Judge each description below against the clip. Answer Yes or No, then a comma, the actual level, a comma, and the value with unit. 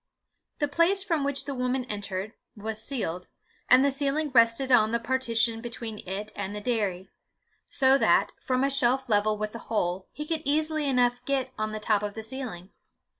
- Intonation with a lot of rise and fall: No, average, 4.3 semitones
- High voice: Yes, high, 240 Hz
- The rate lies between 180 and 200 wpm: Yes, average, 185 wpm